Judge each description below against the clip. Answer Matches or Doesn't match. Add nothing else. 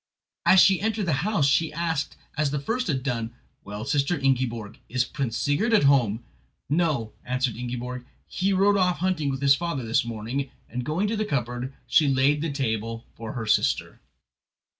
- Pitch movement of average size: Doesn't match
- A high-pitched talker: Doesn't match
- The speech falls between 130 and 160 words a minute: Doesn't match